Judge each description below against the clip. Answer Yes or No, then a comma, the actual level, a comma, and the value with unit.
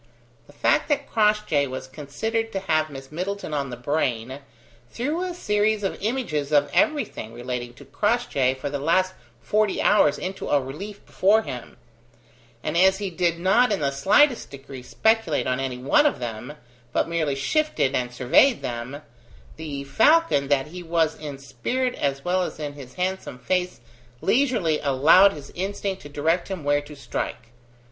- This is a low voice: No, medium, 155 Hz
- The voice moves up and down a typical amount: No, wide, 6.8 semitones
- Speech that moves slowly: No, average, 165 wpm